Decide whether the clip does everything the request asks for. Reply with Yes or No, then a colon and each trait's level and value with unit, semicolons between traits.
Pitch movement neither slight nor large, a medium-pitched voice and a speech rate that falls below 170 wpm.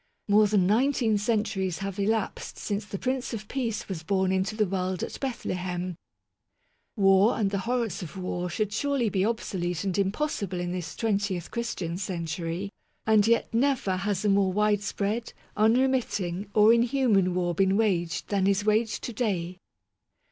No: average, 3.2 semitones; high, 200 Hz; average, 155 wpm